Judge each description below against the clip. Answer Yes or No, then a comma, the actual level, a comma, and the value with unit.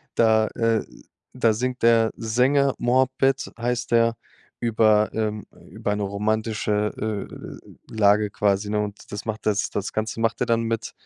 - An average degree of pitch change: No, narrow, 1.8 semitones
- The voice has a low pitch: Yes, low, 110 Hz